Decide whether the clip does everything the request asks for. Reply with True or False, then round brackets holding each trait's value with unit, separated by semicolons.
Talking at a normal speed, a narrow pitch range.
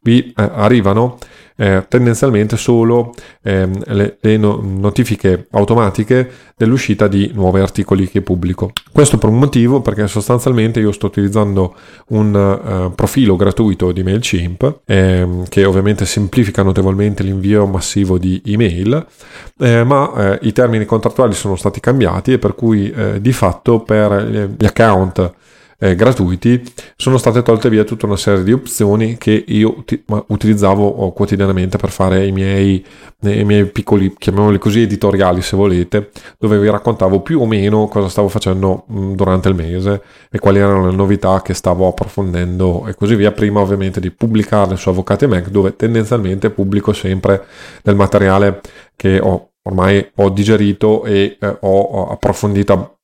True (150 wpm; 2.3 semitones)